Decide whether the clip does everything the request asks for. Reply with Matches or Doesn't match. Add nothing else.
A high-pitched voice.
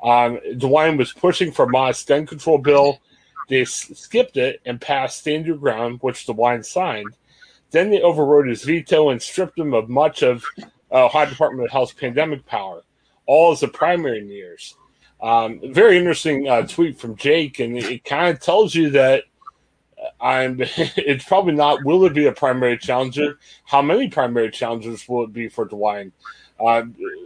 Doesn't match